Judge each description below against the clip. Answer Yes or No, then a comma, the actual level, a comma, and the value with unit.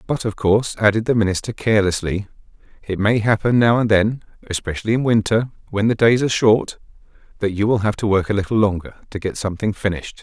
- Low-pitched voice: Yes, low, 105 Hz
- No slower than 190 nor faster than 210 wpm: Yes, average, 200 wpm